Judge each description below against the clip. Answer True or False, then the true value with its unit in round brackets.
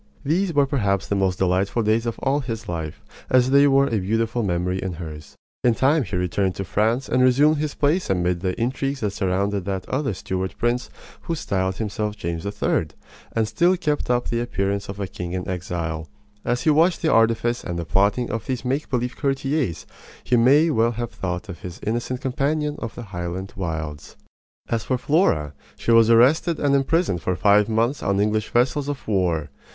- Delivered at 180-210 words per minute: True (195 wpm)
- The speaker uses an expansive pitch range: True (6.0 semitones)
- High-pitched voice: False (115 Hz)